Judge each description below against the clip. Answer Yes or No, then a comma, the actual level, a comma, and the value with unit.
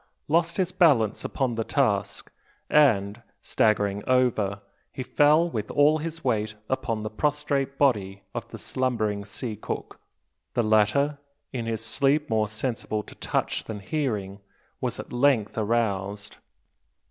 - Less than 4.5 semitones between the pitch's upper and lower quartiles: No, average, 5.1 semitones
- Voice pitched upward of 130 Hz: No, low, 115 Hz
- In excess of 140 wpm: No, slow, 135 wpm